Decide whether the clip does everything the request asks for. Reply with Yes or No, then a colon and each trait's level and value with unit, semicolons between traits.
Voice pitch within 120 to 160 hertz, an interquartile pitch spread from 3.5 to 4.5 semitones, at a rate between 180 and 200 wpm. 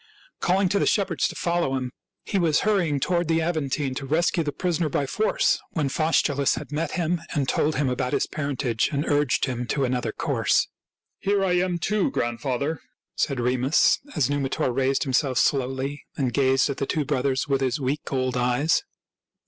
Yes: medium, 140 Hz; average, 3.8 semitones; average, 190 wpm